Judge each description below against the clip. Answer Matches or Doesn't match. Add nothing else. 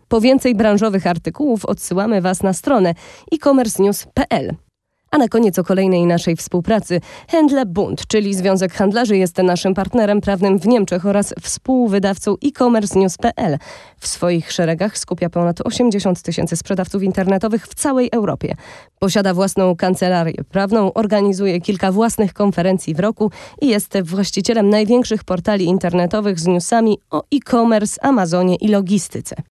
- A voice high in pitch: Matches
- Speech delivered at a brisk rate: Doesn't match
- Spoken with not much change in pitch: Doesn't match